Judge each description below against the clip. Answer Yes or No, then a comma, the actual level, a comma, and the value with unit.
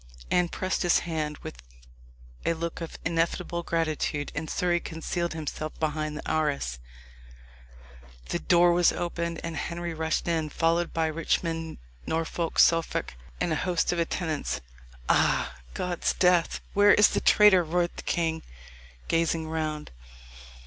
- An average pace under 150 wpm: Yes, slow, 135 wpm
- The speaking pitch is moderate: Yes, medium, 165 Hz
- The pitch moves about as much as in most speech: No, narrow, 1.5 semitones